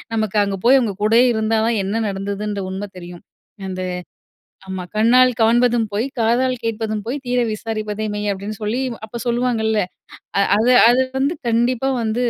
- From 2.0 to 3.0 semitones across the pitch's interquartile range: Yes, narrow, 2.5 semitones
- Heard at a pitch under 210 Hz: No, high, 220 Hz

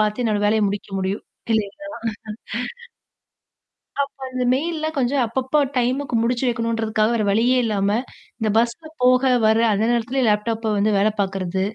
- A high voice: Yes, high, 225 Hz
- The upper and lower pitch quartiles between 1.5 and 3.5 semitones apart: Yes, average, 3.2 semitones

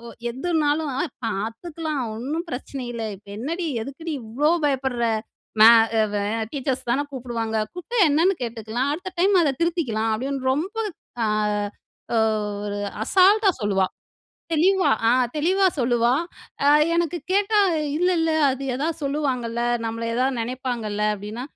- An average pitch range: No, wide, 6.1 semitones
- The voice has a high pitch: Yes, very high, 270 Hz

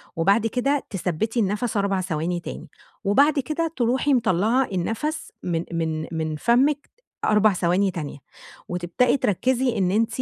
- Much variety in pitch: Yes, wide, 6.2 semitones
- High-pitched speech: Yes, high, 210 Hz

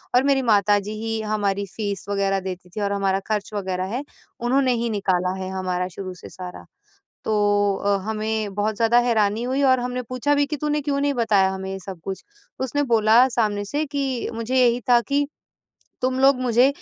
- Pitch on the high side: Yes, high, 215 Hz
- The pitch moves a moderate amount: Yes, average, 4.1 semitones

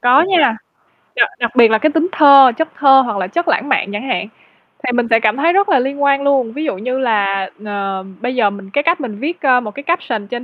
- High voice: Yes, very high, 255 Hz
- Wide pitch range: No, average, 4.7 semitones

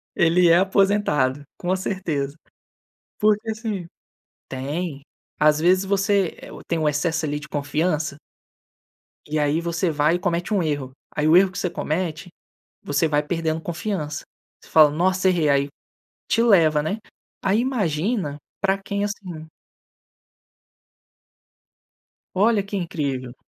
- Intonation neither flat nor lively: Yes, average, 4.3 semitones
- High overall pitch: No, medium, 170 Hz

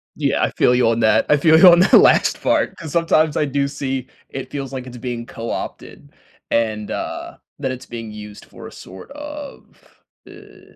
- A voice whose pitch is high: No, low, 130 Hz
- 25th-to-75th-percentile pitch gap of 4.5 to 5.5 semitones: Yes, average, 5.2 semitones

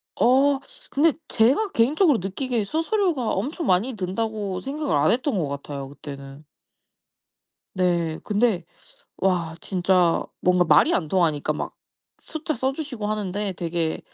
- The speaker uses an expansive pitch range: Yes, wide, 7.5 semitones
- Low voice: No, high, 205 Hz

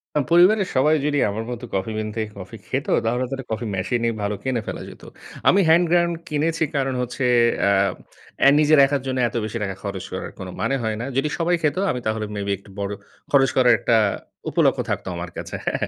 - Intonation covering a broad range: Yes, wide, 5.7 semitones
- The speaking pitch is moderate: No, low, 125 Hz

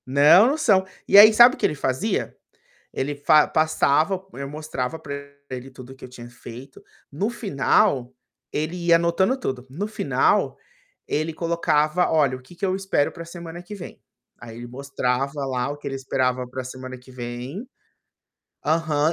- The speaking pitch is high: No, medium, 145 Hz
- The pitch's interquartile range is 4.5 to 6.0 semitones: Yes, average, 4.9 semitones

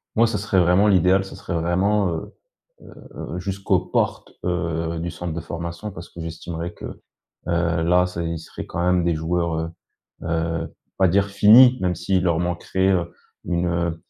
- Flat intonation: Yes, narrow, 2.1 semitones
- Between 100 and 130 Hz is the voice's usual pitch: No, very low, 85 Hz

